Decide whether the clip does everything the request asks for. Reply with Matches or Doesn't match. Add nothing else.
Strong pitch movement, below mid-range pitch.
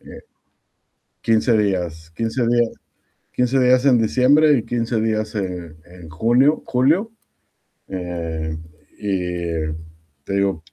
Matches